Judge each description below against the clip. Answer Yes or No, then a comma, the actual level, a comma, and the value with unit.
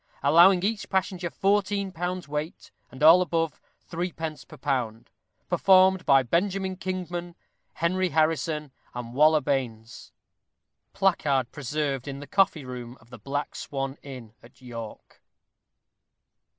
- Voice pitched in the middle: Yes, medium, 155 Hz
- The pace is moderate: No, slow, 125 wpm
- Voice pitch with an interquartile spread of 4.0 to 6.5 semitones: Yes, average, 5.3 semitones